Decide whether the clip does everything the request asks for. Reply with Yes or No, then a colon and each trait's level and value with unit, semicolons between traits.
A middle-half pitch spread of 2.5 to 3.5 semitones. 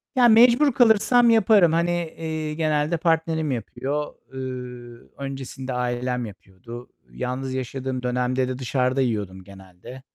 No: average, 4.6 semitones